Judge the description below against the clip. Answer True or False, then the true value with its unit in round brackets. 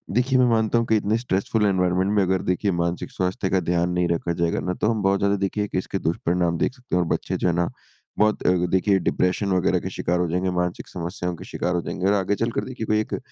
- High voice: False (95 Hz)